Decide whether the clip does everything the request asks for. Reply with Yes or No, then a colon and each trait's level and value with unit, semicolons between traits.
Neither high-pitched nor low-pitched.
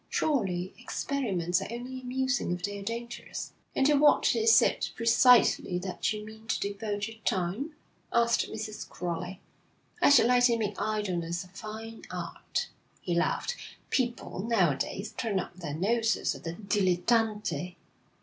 No: high, 215 Hz